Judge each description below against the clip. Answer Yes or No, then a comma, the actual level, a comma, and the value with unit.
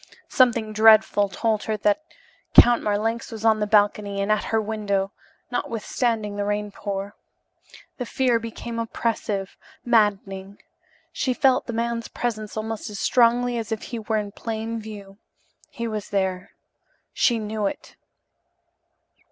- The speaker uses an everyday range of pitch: No, narrow, 2.1 semitones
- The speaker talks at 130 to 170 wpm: Yes, average, 140 wpm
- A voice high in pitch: Yes, high, 215 Hz